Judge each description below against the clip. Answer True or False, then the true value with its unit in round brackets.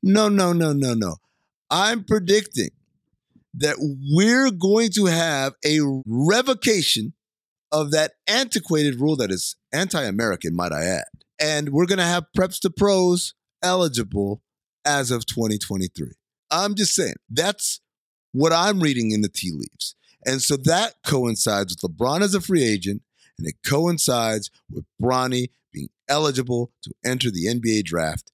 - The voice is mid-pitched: True (150 Hz)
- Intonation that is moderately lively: False (7.4 semitones)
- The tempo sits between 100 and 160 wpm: True (150 wpm)